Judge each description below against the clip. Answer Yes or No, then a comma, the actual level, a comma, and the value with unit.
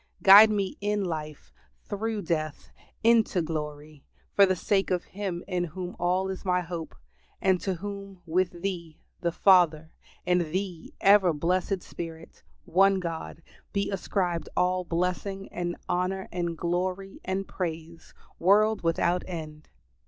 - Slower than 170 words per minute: Yes, slow, 135 wpm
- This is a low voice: No, medium, 180 Hz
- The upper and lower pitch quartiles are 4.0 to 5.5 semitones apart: No, narrow, 2.5 semitones